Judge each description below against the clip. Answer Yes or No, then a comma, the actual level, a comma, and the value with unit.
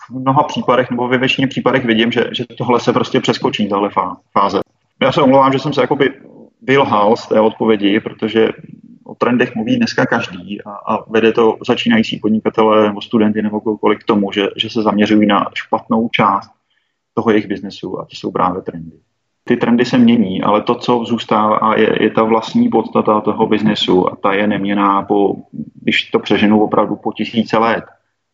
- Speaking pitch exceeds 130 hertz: No, low, 110 Hz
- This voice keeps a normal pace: No, fast, 185 wpm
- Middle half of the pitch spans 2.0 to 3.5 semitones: Yes, average, 2.8 semitones